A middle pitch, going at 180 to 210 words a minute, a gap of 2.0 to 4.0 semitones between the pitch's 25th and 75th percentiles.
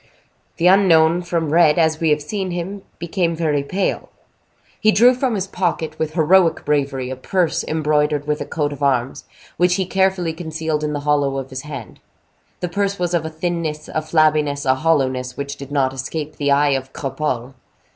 Yes: medium, 155 Hz; average, 185 wpm; average, 3.4 semitones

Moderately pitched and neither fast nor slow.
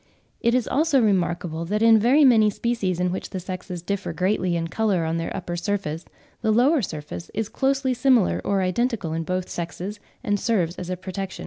No: high, 195 Hz; average, 195 wpm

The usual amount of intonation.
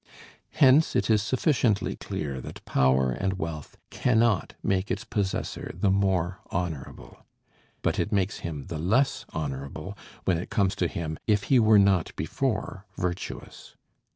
Yes: average, 4.8 semitones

